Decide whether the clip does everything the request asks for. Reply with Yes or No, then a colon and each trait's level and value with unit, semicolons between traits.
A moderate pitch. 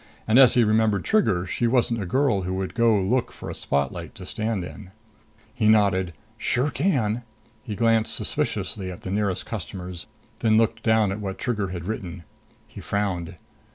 No: low, 105 Hz